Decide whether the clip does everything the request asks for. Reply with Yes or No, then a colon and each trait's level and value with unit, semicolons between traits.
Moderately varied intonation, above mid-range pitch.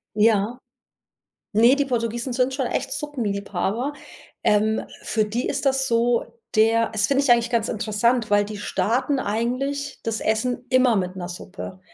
Yes: average, 3.3 semitones; high, 230 Hz